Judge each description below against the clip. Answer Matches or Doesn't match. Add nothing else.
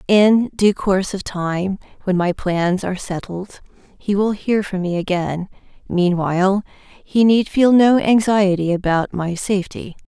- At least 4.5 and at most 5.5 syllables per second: Doesn't match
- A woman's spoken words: Matches